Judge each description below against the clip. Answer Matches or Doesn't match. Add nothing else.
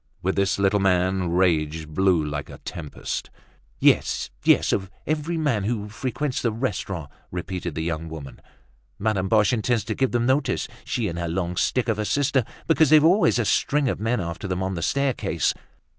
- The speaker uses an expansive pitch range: Matches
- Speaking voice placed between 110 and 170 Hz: Doesn't match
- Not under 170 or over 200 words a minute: Matches